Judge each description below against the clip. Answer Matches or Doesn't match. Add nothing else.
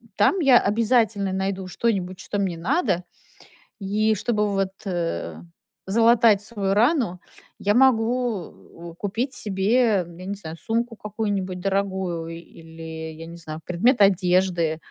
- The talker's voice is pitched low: Doesn't match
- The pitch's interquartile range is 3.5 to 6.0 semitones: Matches